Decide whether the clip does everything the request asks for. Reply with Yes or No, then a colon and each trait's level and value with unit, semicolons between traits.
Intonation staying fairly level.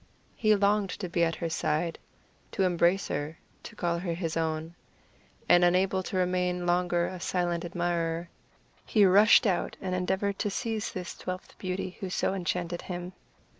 Yes: narrow, 1.7 semitones